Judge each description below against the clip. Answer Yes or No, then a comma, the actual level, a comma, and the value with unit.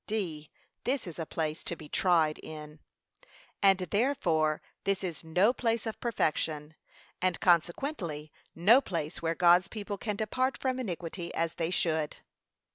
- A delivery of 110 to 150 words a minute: Yes, average, 145 wpm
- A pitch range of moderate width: Yes, average, 5.0 semitones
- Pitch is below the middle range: No, medium, 175 Hz